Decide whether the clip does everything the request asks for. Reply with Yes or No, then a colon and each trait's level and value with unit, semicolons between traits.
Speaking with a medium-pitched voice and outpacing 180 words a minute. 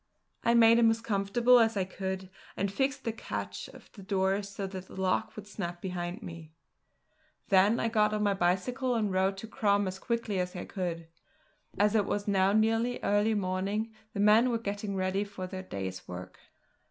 No: high, 200 Hz; average, 190 wpm